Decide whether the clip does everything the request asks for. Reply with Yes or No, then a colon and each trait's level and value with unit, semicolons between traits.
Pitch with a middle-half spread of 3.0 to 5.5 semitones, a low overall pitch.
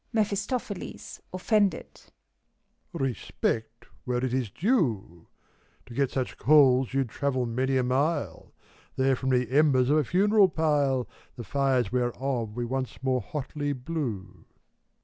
Yes: average, 3.5 semitones; low, 130 Hz